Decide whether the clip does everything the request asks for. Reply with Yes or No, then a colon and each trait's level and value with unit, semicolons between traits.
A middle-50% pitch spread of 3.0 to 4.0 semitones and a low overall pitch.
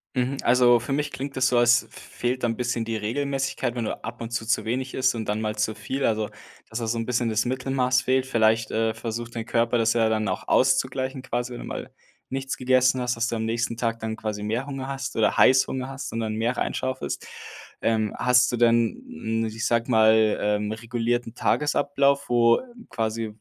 No: narrow, 2.5 semitones; low, 120 Hz